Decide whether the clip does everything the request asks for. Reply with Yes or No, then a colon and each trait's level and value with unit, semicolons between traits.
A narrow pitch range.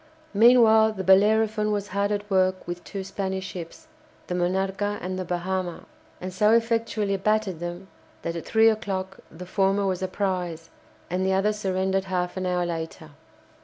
Yes: narrow, 2.3 semitones